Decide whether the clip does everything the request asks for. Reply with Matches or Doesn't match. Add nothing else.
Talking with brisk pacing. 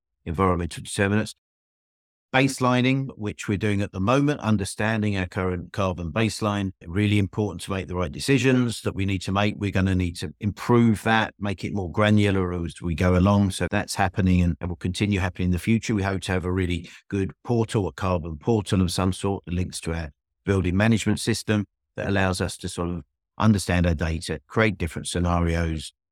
Doesn't match